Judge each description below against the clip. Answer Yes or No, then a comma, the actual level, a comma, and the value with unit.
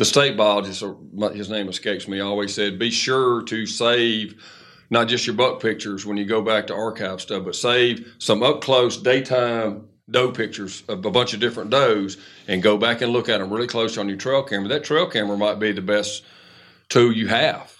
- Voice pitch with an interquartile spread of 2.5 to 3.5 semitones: Yes, average, 2.8 semitones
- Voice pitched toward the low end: Yes, low, 110 Hz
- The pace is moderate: No, fast, 210 wpm